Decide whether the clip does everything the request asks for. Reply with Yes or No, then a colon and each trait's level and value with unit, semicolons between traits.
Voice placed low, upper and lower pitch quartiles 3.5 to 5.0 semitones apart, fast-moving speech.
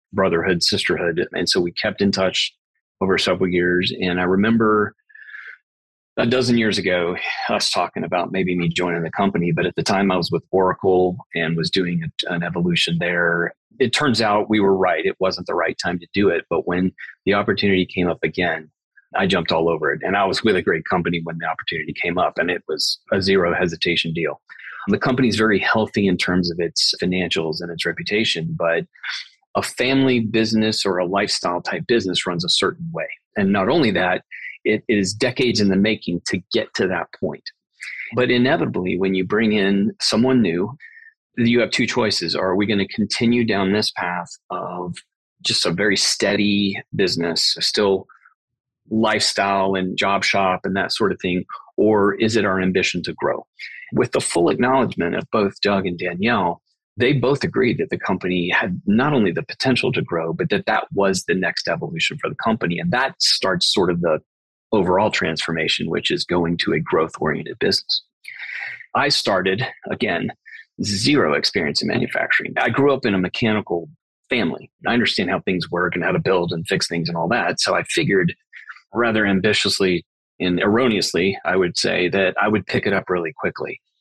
No: very low, 95 Hz; average, 3.8 semitones; average, 190 wpm